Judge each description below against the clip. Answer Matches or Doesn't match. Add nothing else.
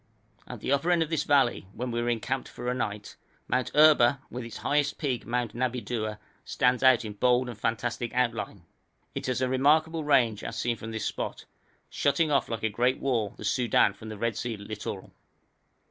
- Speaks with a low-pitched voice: Matches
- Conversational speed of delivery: Matches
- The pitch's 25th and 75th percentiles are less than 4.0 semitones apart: Matches